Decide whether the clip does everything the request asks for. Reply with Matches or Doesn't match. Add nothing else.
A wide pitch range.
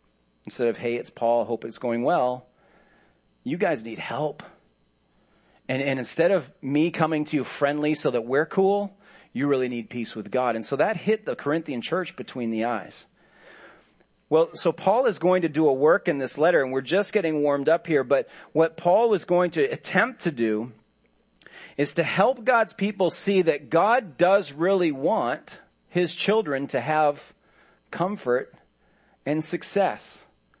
Matches